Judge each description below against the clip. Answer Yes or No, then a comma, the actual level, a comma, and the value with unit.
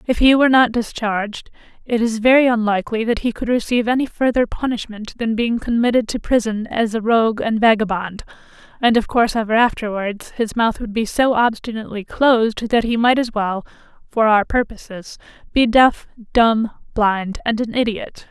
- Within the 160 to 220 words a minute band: Yes, average, 175 wpm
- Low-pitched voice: No, high, 225 Hz